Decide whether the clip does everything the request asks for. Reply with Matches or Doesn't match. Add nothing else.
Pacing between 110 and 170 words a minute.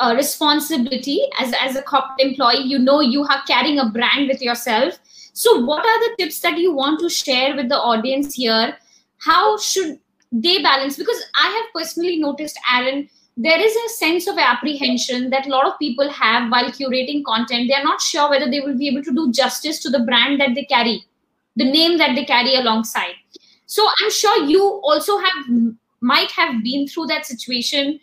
Doesn't match